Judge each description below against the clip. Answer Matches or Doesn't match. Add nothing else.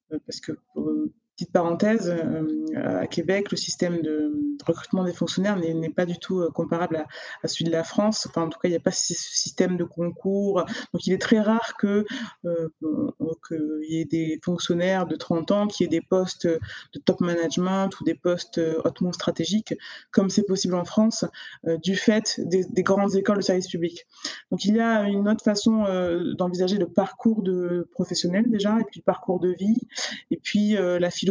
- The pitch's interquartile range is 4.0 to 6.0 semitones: Doesn't match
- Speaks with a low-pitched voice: Doesn't match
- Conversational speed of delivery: Matches